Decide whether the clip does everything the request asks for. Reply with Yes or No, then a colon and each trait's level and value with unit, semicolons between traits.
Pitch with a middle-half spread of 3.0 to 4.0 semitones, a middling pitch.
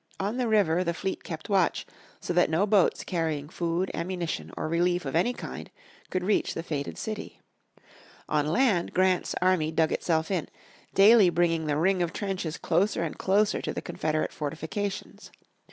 Yes: average, 3.3 semitones; medium, 175 Hz